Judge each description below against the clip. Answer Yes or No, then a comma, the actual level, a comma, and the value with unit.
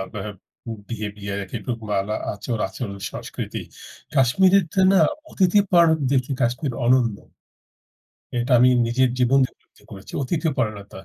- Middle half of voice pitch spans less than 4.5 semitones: No, average, 5.1 semitones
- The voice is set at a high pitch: No, low, 120 Hz